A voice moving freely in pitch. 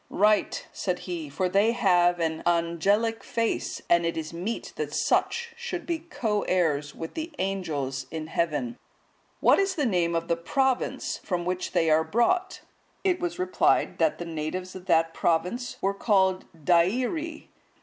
Yes: wide, 6.3 semitones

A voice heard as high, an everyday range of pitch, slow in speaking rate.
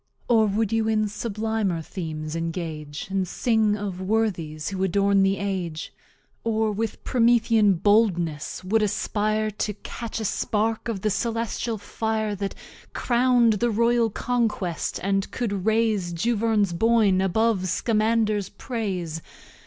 Yes: high, 210 Hz; average, 3.0 semitones; slow, 130 wpm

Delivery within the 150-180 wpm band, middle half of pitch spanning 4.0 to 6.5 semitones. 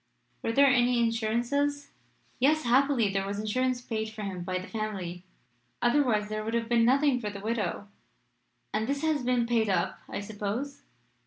No: average, 170 wpm; average, 3.4 semitones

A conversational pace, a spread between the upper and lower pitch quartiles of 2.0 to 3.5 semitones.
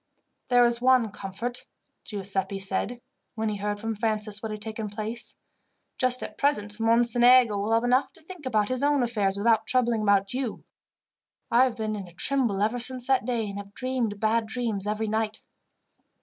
Yes: average, 180 wpm; average, 2.9 semitones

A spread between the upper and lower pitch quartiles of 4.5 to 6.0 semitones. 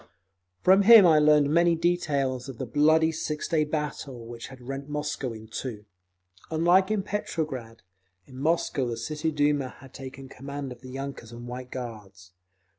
No: average, 3.9 semitones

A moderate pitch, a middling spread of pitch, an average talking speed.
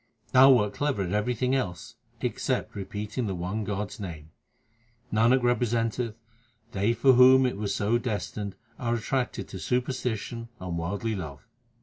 No: low, 110 Hz; average, 3.8 semitones; average, 145 wpm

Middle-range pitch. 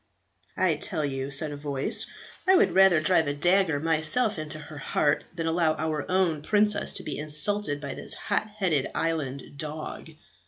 Yes: medium, 155 Hz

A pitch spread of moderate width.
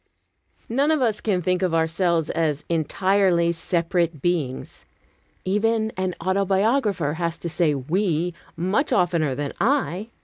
Yes: average, 3.4 semitones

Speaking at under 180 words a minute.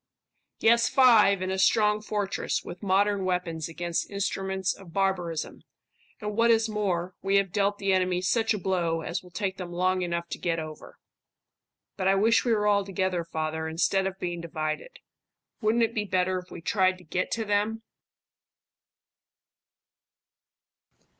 Yes: average, 160 wpm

